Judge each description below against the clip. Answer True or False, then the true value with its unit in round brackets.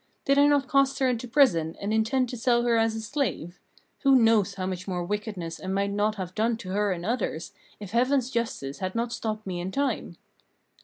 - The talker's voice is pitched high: True (220 Hz)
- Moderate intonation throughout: True (4.7 semitones)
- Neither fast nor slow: False (215 wpm)